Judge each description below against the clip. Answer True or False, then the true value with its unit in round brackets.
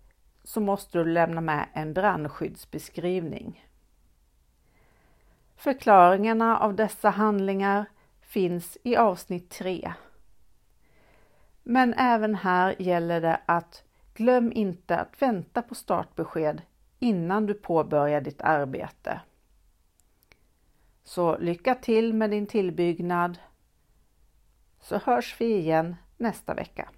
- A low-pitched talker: False (180 Hz)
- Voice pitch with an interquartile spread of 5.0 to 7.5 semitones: True (5.3 semitones)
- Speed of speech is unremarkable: False (100 wpm)